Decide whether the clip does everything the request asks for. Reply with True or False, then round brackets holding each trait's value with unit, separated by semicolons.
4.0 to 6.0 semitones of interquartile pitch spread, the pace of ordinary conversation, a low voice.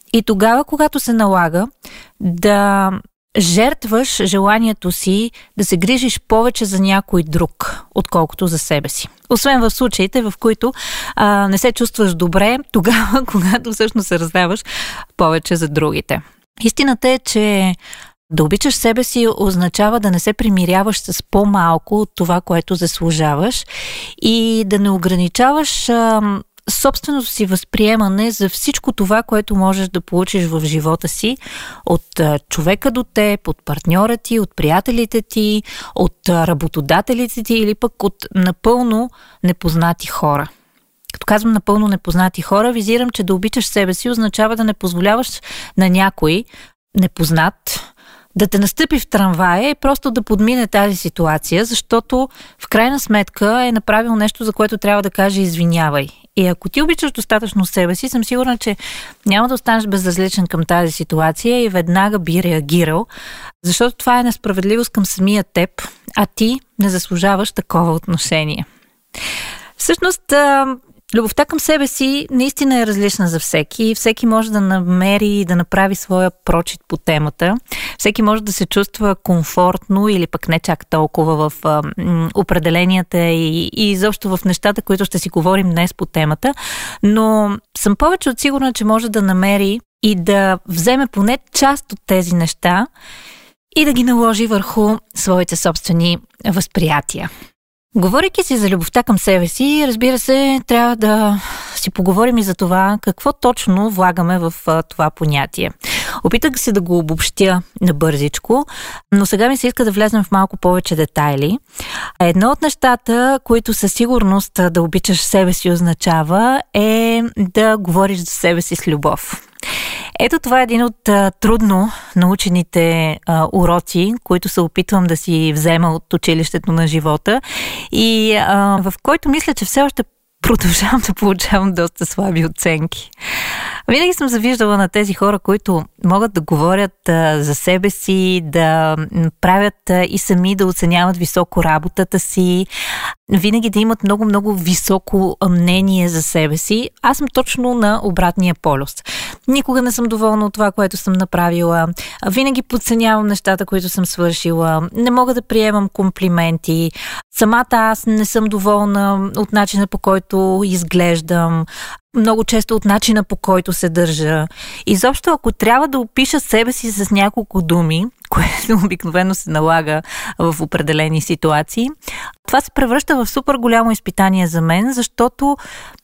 False (4.5 semitones; 150 wpm; 200 Hz)